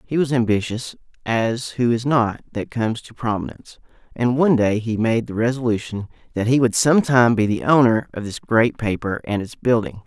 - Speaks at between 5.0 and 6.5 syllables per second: Yes, 5.5 syllables/s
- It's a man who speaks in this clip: Yes, male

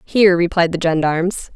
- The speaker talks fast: No, average, 155 wpm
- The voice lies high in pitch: No, medium, 175 Hz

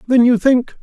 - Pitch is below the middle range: No, high, 245 Hz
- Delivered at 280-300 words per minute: No, fast, 220 wpm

